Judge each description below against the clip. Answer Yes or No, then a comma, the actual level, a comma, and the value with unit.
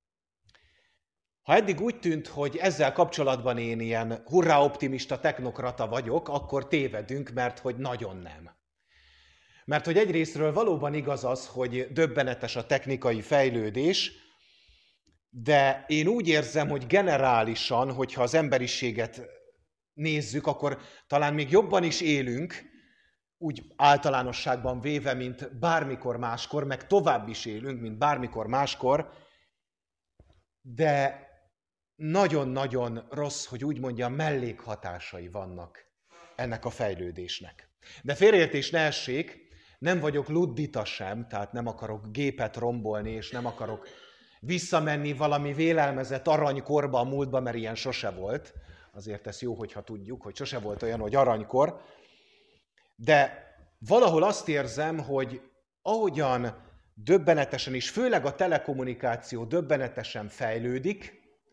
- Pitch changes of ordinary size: Yes, average, 4.1 semitones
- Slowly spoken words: Yes, slow, 115 wpm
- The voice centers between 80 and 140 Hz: Yes, low, 135 Hz